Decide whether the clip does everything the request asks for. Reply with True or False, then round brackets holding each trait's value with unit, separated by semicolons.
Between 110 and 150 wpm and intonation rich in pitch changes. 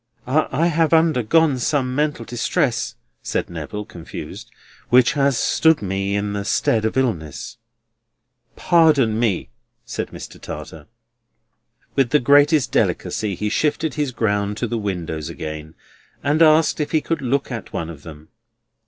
True (145 wpm; 6.7 semitones)